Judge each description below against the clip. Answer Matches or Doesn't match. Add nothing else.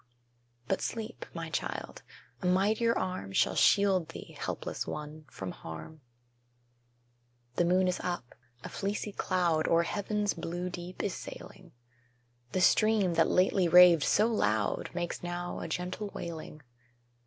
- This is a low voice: Doesn't match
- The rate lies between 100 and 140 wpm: Matches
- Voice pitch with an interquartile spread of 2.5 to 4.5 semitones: Matches